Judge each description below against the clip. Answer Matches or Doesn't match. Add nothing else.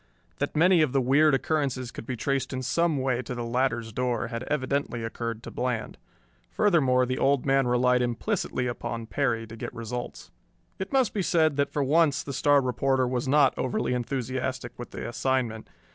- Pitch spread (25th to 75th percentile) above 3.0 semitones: Doesn't match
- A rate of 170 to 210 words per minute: Matches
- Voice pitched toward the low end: Matches